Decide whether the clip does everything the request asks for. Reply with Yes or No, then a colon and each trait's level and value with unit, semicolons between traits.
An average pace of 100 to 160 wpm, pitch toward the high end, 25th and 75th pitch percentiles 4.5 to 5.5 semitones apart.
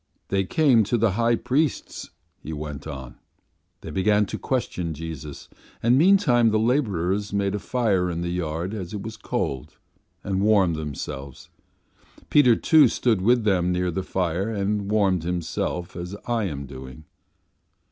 No: average, 155 wpm; very low, 95 Hz; average, 4.9 semitones